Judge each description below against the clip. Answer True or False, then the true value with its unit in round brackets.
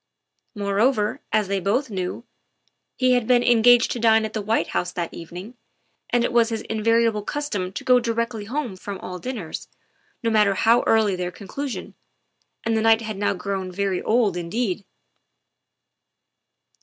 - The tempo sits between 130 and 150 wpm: False (165 wpm)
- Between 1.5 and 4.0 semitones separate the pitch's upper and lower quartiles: True (3.0 semitones)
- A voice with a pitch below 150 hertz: False (220 Hz)